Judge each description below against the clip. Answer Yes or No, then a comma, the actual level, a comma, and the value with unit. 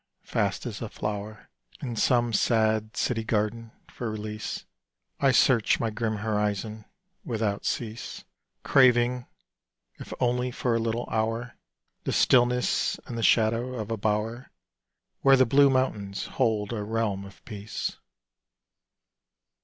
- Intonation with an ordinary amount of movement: No, narrow, 2.3 semitones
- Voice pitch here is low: Yes, low, 115 Hz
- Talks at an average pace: No, slow, 130 wpm